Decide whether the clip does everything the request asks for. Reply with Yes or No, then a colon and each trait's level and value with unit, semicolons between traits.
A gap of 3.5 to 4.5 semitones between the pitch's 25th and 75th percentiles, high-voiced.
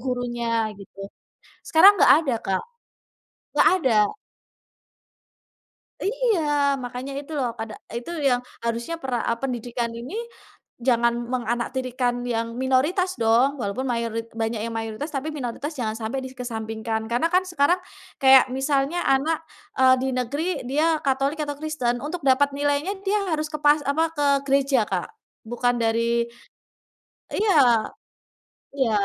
Yes: average, 3.8 semitones; very high, 255 Hz